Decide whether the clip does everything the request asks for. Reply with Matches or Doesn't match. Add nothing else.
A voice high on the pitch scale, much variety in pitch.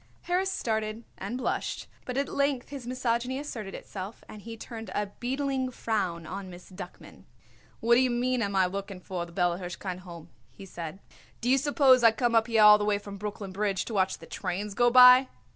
Doesn't match